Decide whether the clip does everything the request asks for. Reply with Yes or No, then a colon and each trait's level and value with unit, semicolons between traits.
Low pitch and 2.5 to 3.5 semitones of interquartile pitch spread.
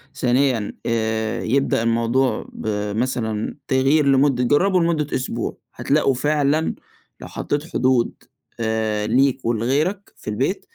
No: low, 130 Hz; average, 4.0 semitones